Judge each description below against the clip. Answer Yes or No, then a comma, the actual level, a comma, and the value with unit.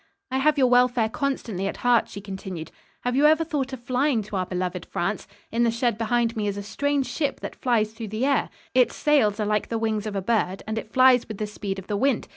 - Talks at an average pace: No, fast, 250 wpm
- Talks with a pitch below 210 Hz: No, high, 225 Hz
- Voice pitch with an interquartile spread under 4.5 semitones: Yes, average, 4.0 semitones